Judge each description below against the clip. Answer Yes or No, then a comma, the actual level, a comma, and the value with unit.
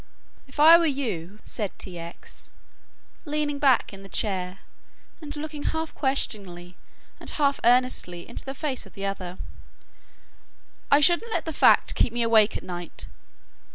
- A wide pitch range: Yes, wide, 7.3 semitones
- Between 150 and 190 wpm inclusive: Yes, average, 155 wpm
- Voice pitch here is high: Yes, high, 240 Hz